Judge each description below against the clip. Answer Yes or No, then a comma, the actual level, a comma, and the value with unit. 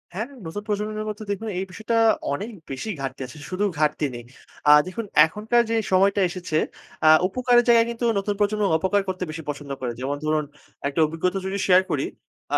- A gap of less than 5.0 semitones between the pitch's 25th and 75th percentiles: No, wide, 5.5 semitones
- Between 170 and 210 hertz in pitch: Yes, high, 190 Hz